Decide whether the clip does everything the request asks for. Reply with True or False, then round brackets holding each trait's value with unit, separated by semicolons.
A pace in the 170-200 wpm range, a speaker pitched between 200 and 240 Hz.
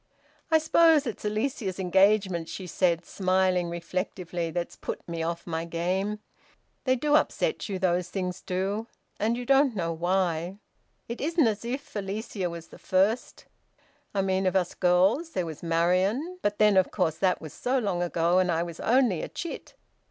False (175 wpm; 190 Hz)